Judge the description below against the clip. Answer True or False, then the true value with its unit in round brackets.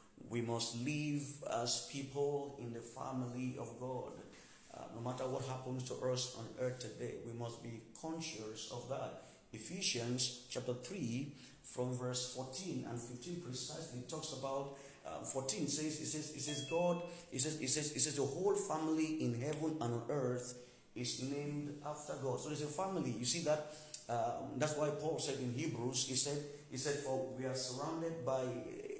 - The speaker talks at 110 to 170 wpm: False (180 wpm)